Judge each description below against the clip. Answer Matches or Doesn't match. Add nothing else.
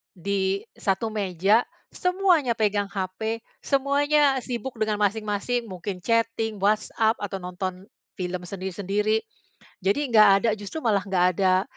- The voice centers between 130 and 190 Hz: Doesn't match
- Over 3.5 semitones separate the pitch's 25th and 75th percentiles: Doesn't match